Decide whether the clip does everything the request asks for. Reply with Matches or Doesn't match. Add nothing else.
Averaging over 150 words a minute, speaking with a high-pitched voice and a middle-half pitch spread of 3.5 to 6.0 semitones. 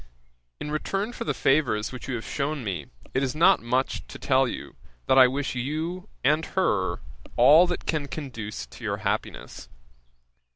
Doesn't match